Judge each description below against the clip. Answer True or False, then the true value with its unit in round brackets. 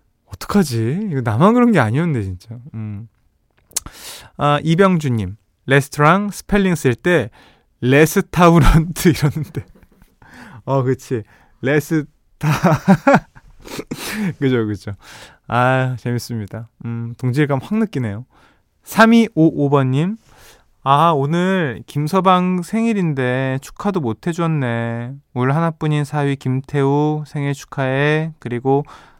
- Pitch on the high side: False (140 Hz)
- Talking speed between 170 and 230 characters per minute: True (220 characters per minute)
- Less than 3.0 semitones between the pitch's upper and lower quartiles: False (5.5 semitones)